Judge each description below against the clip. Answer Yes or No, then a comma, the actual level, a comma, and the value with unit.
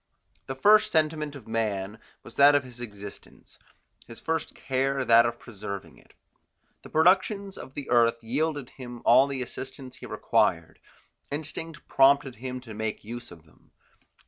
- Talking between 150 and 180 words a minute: Yes, average, 155 wpm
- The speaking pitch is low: Yes, low, 130 Hz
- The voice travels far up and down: No, average, 4.3 semitones